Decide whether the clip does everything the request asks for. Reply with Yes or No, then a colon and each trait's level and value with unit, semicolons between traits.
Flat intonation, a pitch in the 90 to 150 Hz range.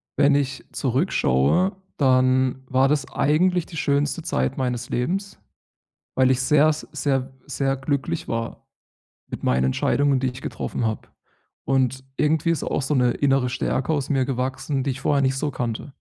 Yes: narrow, 2.3 semitones; low, 135 Hz